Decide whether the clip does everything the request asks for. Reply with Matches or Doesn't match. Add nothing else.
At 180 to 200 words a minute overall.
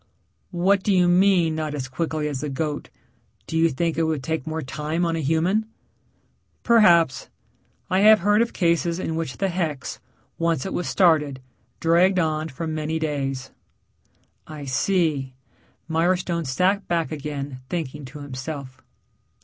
Doesn't match